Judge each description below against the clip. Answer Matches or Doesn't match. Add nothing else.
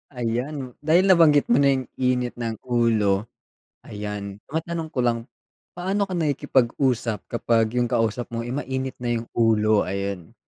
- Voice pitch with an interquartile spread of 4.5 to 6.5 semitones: Doesn't match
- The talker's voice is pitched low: Matches